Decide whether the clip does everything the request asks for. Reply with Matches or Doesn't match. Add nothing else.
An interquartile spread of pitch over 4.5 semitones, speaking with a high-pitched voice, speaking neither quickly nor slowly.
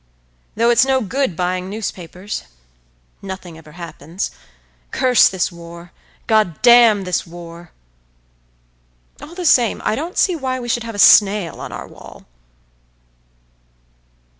Doesn't match